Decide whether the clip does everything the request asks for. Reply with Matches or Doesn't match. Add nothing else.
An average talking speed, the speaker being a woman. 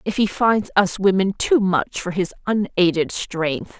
Matches